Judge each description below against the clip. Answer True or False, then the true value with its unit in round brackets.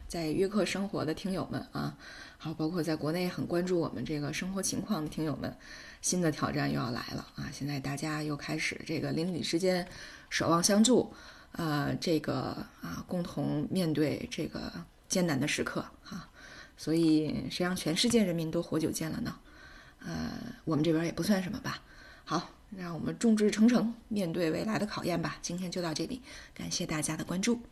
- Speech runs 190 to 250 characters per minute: False (280 characters per minute)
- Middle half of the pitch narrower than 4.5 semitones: True (3.4 semitones)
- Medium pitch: True (170 Hz)